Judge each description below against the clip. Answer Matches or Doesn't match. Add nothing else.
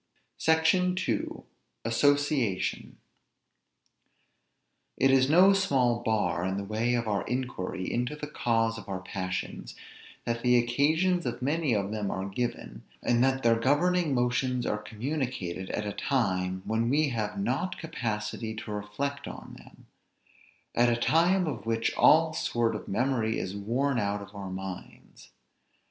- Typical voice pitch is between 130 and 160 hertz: Doesn't match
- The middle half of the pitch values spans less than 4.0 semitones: Doesn't match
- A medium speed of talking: Matches